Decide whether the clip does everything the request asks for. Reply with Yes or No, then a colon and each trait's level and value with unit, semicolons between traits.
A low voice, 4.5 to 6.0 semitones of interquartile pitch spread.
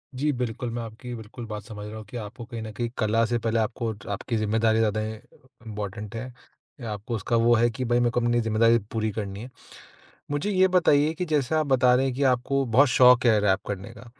No: low, 115 Hz; narrow, 2.6 semitones